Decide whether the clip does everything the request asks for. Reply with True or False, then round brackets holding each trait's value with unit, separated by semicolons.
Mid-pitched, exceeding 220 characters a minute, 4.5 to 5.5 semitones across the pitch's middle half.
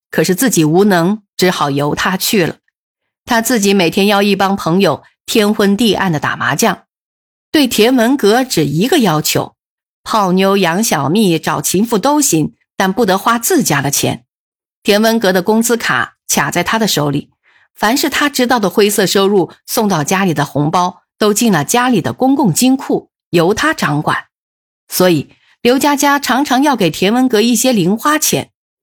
False (200 Hz; 250 characters per minute; 5.2 semitones)